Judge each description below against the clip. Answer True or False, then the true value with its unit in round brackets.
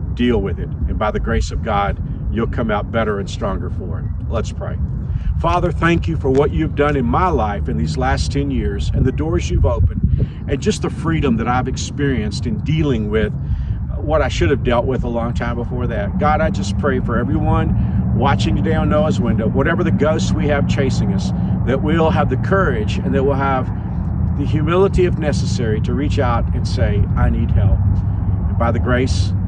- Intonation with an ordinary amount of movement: True (3.7 semitones)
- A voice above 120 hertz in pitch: False (100 Hz)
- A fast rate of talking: True (210 wpm)